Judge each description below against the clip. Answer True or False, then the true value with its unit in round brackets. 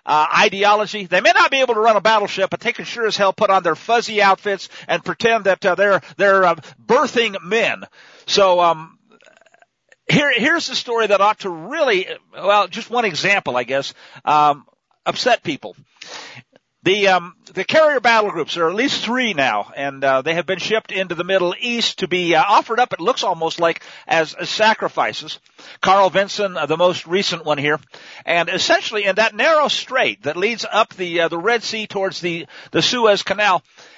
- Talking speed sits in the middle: True (195 wpm)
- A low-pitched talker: False (195 Hz)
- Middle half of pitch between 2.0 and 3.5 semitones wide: False (4.6 semitones)